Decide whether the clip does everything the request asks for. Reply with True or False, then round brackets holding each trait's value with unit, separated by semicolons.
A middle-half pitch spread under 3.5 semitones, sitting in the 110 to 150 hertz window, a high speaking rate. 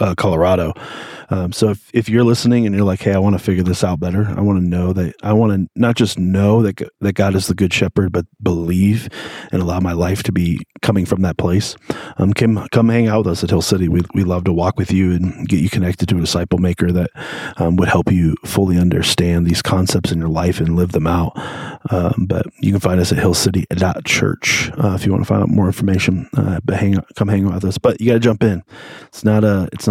False (3.0 semitones; 95 Hz; 255 wpm)